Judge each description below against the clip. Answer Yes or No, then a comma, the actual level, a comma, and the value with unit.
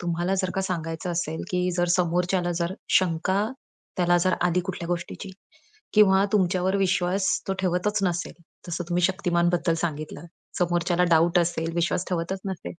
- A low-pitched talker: No, medium, 175 Hz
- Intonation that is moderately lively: No, narrow, 1.5 semitones